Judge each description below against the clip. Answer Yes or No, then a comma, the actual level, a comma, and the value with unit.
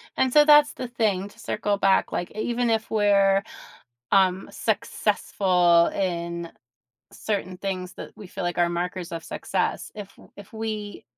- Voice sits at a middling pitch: No, high, 195 Hz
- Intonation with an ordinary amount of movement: Yes, average, 3.2 semitones